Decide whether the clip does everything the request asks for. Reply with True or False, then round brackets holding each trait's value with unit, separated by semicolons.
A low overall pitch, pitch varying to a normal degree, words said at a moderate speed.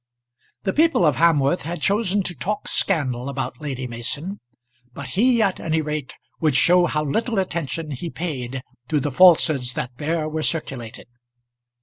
False (155 Hz; 4.7 semitones; 155 wpm)